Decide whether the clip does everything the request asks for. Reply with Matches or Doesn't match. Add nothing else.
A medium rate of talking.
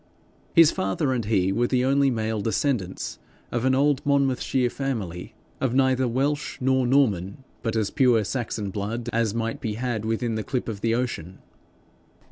Matches